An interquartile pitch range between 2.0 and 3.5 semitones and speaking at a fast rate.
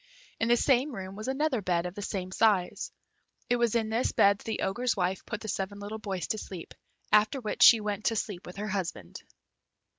Yes: average, 3.1 semitones; fast, 215 wpm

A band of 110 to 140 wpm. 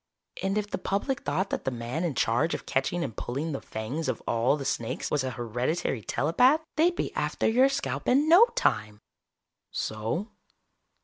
No: average, 180 wpm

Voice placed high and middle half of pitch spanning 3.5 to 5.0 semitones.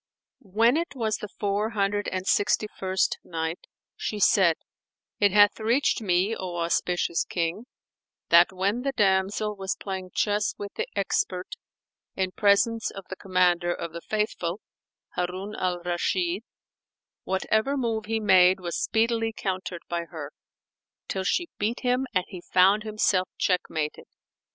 No: high, 195 Hz; average, 3.0 semitones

